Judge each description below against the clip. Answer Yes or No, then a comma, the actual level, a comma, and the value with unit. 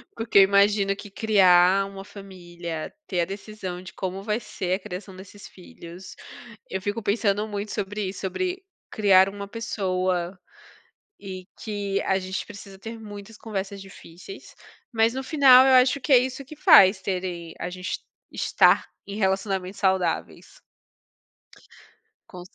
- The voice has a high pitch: Yes, high, 195 Hz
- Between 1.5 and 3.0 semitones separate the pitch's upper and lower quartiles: Yes, narrow, 2.4 semitones